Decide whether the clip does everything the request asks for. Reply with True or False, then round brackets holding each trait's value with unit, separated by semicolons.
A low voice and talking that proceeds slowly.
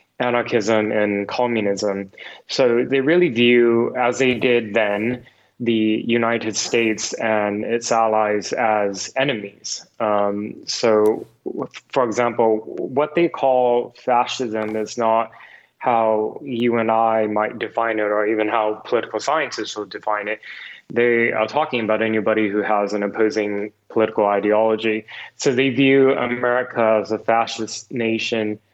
True (110 Hz; 130 wpm)